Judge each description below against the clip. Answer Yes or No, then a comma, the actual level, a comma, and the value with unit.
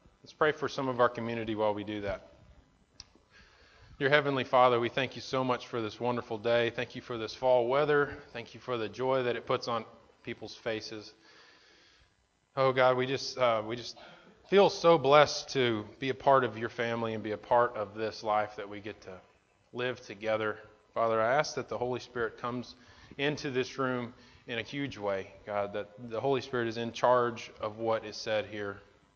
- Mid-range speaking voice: No, low, 120 Hz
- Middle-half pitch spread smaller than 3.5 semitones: Yes, average, 2.9 semitones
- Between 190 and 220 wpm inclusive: Yes, average, 200 wpm